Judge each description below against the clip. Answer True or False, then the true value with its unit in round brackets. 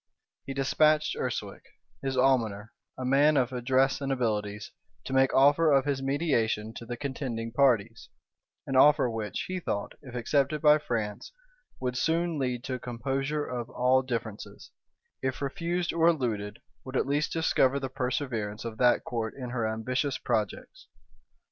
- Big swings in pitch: False (3.3 semitones)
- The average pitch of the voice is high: False (130 Hz)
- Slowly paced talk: False (155 wpm)